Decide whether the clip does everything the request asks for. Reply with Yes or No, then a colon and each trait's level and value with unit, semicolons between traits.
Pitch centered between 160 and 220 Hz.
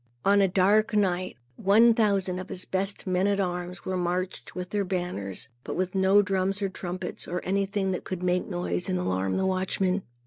Yes: medium, 185 Hz